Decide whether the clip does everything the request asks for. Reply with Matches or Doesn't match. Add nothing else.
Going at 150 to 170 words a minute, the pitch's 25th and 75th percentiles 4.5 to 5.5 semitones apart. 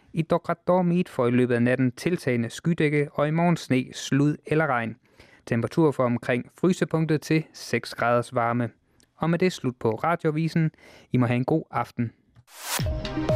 Matches